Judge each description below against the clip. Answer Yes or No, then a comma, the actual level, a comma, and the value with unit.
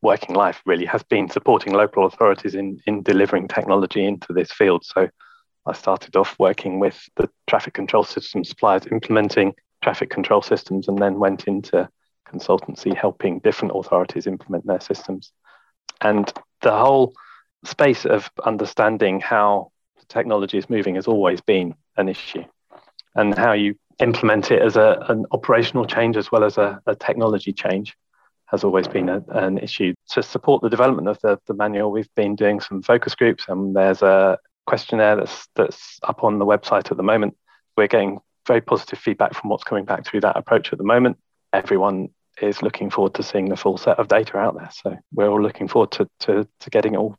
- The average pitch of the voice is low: Yes, low, 100 Hz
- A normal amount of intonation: No, narrow, 1.5 semitones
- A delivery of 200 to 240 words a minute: No, average, 185 wpm